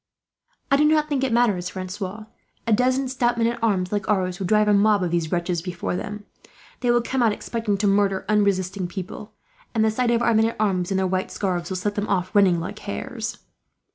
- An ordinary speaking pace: No, fast, 225 wpm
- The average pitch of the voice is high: Yes, high, 205 Hz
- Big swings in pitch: No, average, 3.7 semitones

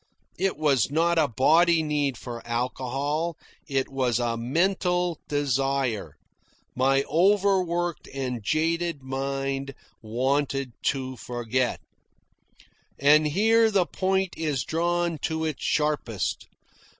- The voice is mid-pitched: Yes, medium, 145 Hz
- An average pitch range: Yes, average, 4.5 semitones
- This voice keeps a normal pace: No, slow, 110 wpm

